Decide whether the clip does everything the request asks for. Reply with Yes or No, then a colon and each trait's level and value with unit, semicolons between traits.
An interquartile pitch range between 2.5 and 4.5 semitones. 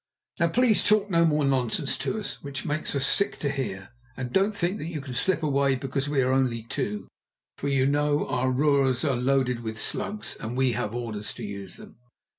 Yes: average, 3.5 semitones